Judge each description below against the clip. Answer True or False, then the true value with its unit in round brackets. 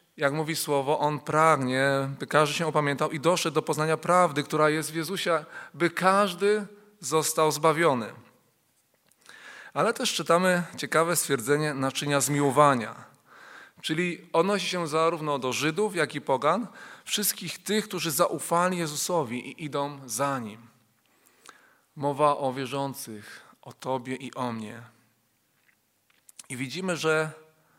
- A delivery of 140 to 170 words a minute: False (125 wpm)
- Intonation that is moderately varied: True (3.5 semitones)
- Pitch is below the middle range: False (155 Hz)